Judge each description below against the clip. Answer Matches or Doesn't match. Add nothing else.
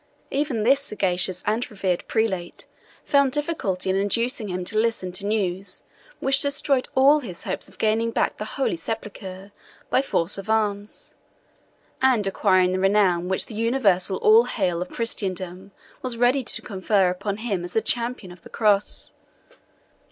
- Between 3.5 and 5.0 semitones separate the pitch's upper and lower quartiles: Matches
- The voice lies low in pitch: Doesn't match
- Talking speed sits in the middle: Matches